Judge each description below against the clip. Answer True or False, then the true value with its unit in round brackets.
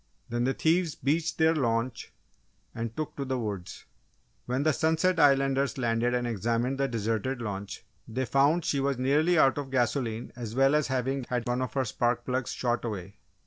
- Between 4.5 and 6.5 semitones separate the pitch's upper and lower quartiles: False (3.0 semitones)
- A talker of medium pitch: False (130 Hz)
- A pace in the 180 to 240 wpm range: True (185 wpm)